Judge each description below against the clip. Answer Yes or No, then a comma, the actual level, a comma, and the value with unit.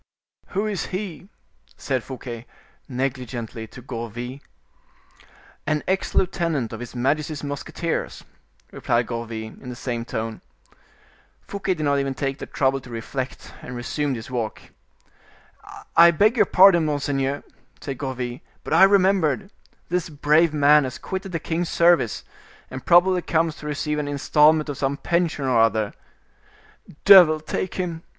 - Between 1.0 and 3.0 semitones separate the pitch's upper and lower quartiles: No, average, 5.1 semitones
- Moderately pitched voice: Yes, medium, 145 Hz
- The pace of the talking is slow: No, average, 145 wpm